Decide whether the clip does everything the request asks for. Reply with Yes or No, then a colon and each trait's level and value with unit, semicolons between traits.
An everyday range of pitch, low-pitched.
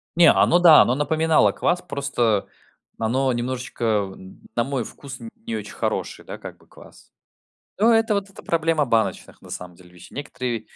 No: wide, 6.3 semitones; low, 130 Hz